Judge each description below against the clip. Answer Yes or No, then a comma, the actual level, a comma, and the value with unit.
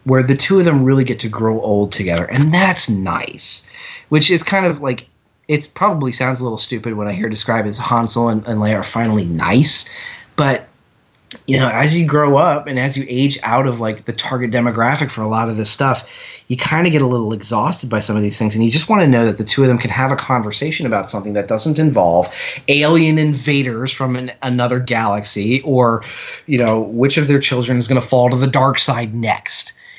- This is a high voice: No, low, 125 Hz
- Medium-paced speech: No, fast, 230 wpm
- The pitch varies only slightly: No, average, 3.9 semitones